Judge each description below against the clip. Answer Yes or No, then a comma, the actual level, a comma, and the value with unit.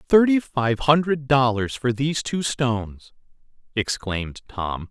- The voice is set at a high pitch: No, low, 130 Hz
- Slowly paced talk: Yes, slow, 120 wpm